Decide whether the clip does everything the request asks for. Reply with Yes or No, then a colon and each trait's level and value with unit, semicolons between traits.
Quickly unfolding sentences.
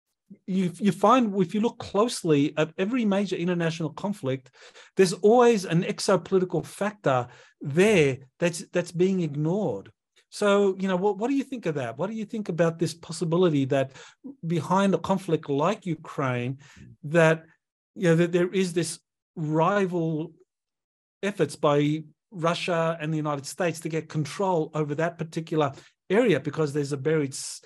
No: average, 155 wpm